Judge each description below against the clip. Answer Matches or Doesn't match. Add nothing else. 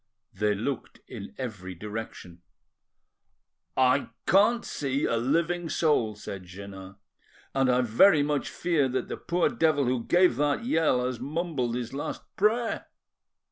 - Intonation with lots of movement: Matches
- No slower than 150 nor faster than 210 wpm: Doesn't match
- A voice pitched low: Matches